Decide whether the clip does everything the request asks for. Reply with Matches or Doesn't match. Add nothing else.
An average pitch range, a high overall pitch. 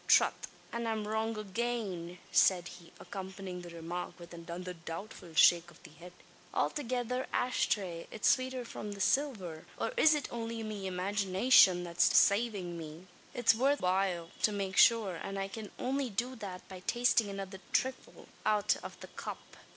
Matches